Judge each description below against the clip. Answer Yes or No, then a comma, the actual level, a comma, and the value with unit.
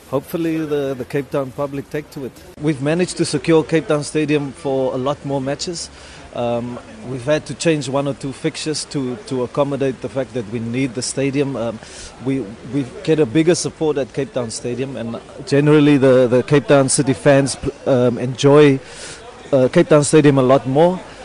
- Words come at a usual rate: Yes, average, 190 wpm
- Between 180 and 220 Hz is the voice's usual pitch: No, medium, 140 Hz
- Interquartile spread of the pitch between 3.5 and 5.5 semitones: No, narrow, 2.5 semitones